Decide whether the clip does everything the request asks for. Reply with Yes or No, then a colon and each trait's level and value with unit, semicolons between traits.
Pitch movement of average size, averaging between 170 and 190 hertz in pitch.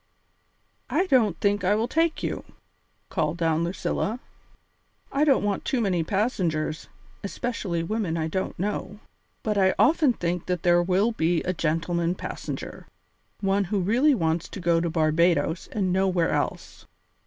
Yes: average, 3.9 semitones; medium, 185 Hz